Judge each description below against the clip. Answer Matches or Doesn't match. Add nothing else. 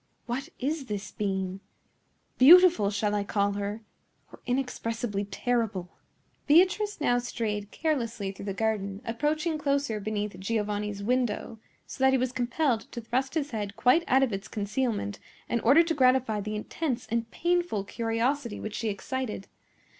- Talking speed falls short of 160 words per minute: Matches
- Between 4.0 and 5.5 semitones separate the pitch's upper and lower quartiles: Matches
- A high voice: Matches